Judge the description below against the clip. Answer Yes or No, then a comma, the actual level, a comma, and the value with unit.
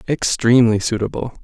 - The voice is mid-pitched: No, low, 115 Hz